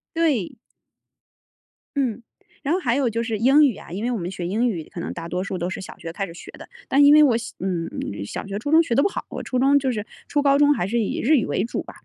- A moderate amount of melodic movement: No, wide, 6.6 semitones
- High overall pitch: Yes, high, 235 Hz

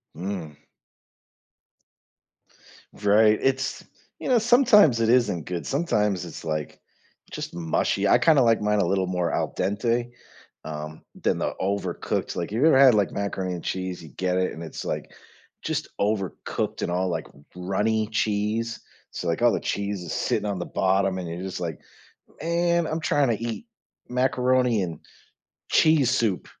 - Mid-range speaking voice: No, low, 100 Hz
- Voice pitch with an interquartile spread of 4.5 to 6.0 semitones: Yes, average, 5.1 semitones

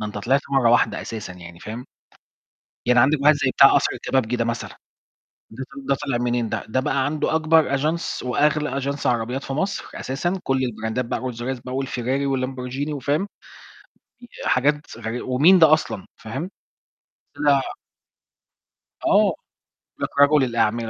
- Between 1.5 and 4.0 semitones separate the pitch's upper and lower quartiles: Yes, average, 3.4 semitones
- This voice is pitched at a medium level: No, low, 130 Hz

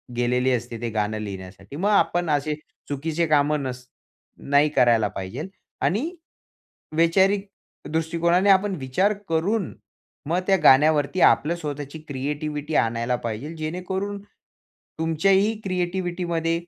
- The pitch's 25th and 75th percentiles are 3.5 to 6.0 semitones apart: Yes, wide, 5.5 semitones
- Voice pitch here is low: No, medium, 155 Hz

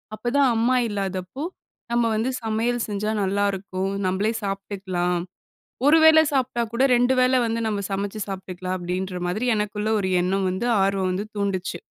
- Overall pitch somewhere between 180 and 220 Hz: Yes, high, 200 Hz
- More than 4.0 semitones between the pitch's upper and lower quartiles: No, average, 3.7 semitones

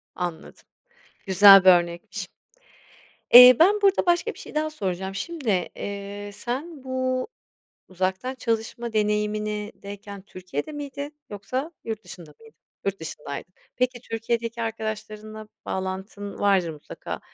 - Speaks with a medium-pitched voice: No, high, 215 Hz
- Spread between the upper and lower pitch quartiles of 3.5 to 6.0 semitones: Yes, average, 4.6 semitones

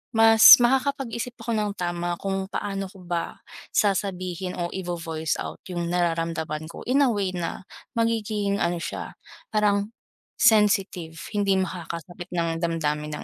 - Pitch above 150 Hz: Yes, medium, 185 Hz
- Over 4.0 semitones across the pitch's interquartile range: No, average, 3.5 semitones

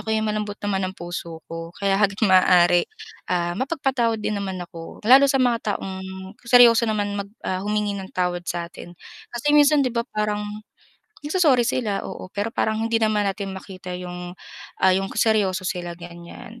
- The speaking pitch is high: Yes, high, 200 Hz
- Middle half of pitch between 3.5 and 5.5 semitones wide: Yes, average, 4.0 semitones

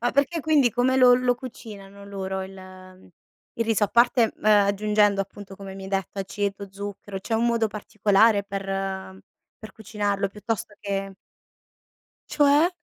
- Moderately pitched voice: No, high, 205 Hz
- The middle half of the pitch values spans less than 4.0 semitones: Yes, average, 2.9 semitones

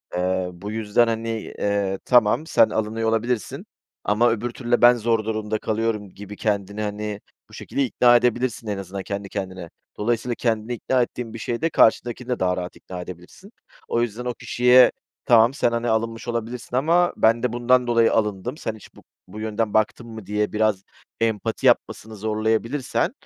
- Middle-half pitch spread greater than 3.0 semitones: No, narrow, 2.4 semitones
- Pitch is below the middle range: Yes, low, 110 Hz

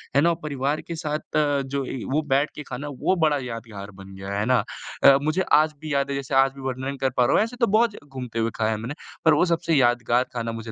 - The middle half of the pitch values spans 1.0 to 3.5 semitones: No, average, 4.2 semitones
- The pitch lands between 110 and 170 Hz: Yes, low, 135 Hz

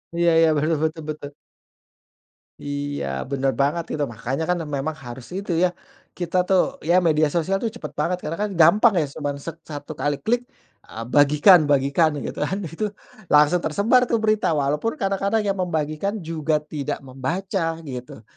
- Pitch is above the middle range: No, medium, 155 Hz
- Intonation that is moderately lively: Yes, average, 4.2 semitones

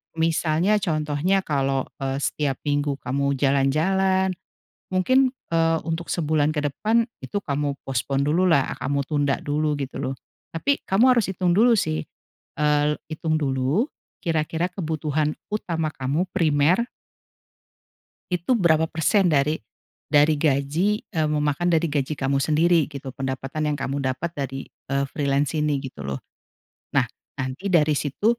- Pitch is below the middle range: No, medium, 150 Hz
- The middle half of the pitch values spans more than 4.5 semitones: No, average, 3.6 semitones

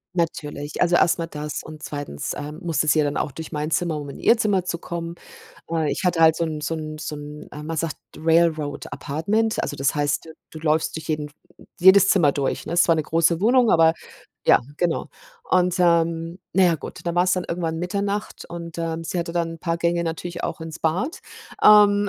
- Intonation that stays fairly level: Yes, narrow, 2.2 semitones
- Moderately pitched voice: Yes, medium, 165 Hz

